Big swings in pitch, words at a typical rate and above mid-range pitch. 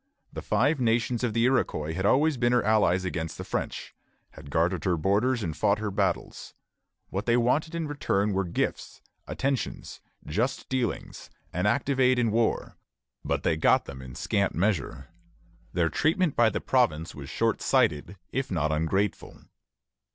No: wide, 6.9 semitones; average, 165 wpm; low, 105 Hz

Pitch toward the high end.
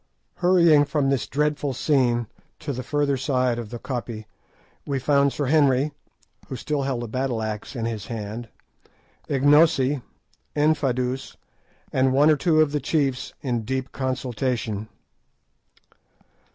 No: low, 135 Hz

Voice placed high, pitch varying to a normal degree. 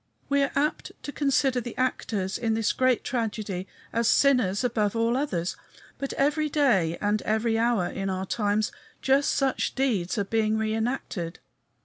Yes: high, 225 Hz; average, 4.5 semitones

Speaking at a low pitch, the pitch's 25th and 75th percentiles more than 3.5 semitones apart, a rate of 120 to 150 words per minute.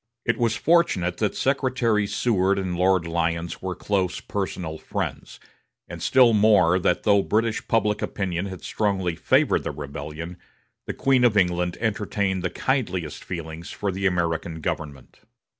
Yes: very low, 95 Hz; average, 3.9 semitones; average, 145 wpm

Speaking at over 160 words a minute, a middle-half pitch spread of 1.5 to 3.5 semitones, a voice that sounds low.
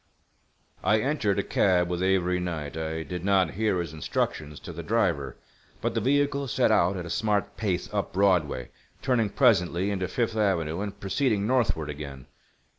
No: average, 170 wpm; average, 4.2 semitones; very low, 95 Hz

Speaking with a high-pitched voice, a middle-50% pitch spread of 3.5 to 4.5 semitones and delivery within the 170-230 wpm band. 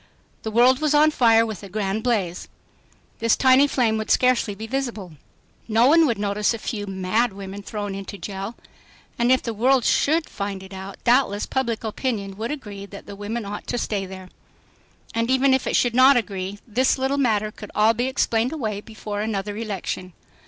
Yes: high, 220 Hz; average, 3.8 semitones; average, 190 wpm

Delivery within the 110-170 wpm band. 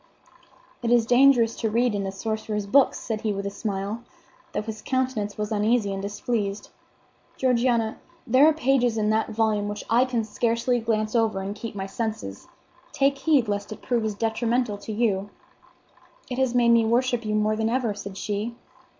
No: average, 185 wpm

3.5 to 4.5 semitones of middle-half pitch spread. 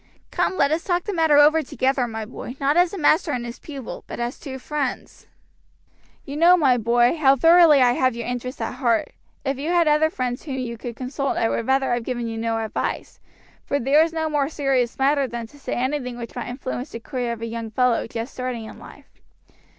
Yes: average, 3.8 semitones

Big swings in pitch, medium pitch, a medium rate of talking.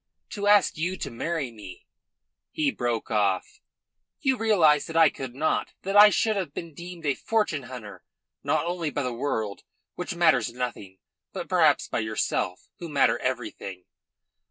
Yes: wide, 7.2 semitones; medium, 150 Hz; average, 165 wpm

